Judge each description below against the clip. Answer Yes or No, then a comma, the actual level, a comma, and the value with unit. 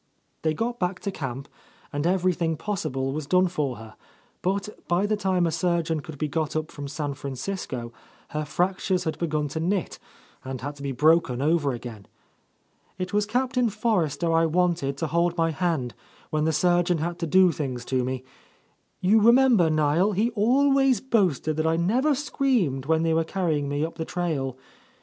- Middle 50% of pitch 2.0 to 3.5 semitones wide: No, average, 4.5 semitones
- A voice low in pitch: No, medium, 165 Hz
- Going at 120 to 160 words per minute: No, average, 180 wpm